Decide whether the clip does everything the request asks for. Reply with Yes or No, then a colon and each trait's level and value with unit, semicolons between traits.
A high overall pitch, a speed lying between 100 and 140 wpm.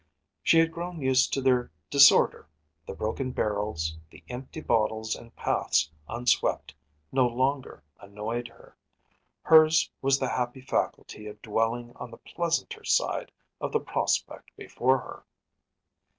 No: low, 125 Hz; slow, 135 wpm